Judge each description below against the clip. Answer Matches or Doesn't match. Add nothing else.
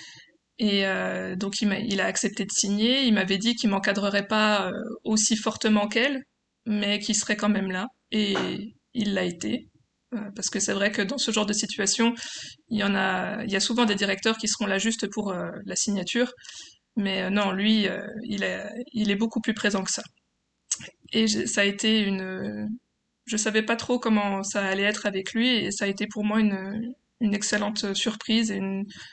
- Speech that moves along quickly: Doesn't match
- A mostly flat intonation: Matches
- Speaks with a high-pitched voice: Matches